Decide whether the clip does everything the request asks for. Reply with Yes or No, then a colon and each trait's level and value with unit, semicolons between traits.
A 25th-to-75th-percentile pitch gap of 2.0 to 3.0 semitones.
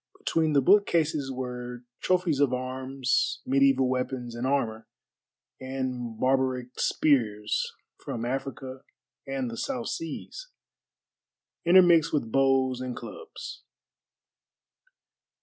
Yes: average, 2.7 semitones